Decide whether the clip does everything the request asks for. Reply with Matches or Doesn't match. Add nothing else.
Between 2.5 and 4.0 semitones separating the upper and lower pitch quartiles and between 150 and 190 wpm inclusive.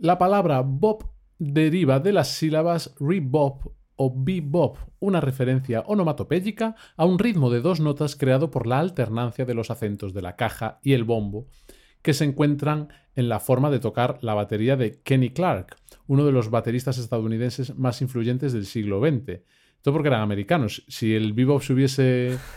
Doesn't match